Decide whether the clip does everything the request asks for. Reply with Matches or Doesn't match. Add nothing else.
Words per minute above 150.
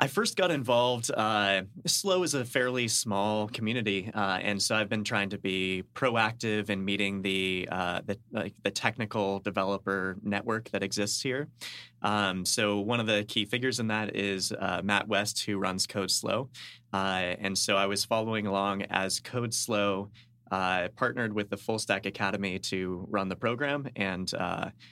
Matches